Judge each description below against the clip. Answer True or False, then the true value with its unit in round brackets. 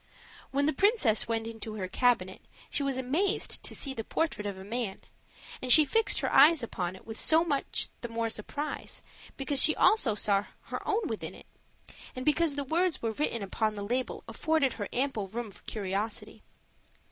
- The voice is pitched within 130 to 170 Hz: False (245 Hz)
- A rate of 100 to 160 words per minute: False (190 wpm)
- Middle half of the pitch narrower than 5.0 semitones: False (5.6 semitones)